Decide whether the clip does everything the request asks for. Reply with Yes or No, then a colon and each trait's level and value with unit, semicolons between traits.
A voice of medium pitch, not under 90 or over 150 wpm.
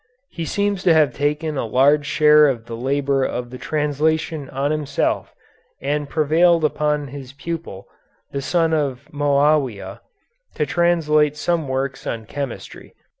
Yes: medium, 145 Hz; average, 140 wpm